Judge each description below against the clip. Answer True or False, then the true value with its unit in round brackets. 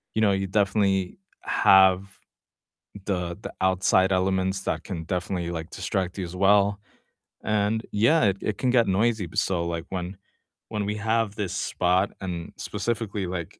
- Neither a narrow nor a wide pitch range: False (2.2 semitones)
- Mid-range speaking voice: False (95 Hz)